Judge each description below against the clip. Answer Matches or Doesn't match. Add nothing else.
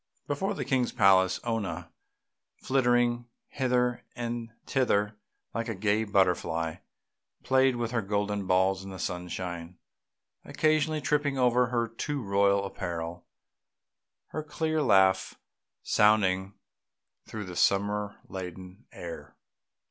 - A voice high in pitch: Doesn't match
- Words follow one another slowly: Matches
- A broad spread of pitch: Doesn't match